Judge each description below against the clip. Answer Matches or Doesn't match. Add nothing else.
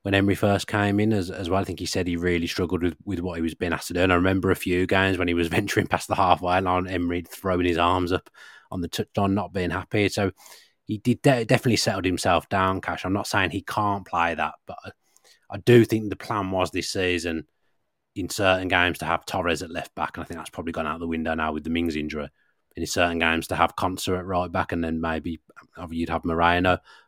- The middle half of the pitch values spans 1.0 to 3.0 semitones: Matches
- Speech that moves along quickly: Matches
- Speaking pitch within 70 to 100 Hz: Matches